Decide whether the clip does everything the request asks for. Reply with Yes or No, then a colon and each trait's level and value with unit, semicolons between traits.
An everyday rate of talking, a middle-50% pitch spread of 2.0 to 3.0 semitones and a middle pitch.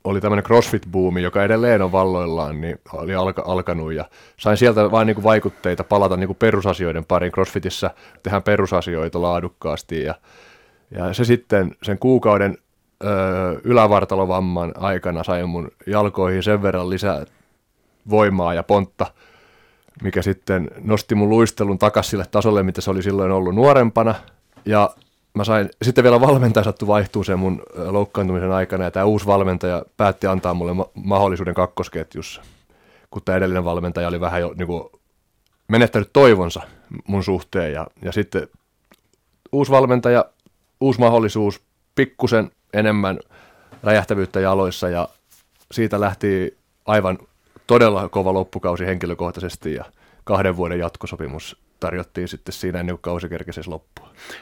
No: average, 130 wpm; average, 2.7 semitones; very low, 95 Hz